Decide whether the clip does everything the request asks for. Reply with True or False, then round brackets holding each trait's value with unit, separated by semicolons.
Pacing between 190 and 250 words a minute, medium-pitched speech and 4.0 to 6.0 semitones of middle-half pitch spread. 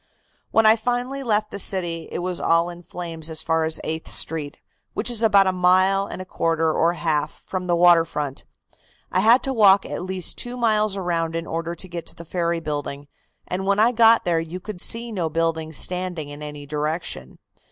False (205 wpm; 175 Hz; 3.6 semitones)